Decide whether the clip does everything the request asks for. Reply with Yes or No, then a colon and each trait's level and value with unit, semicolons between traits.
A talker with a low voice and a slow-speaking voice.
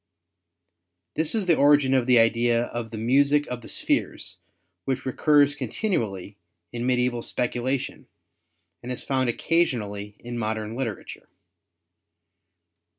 Yes: low, 125 Hz; slow, 120 wpm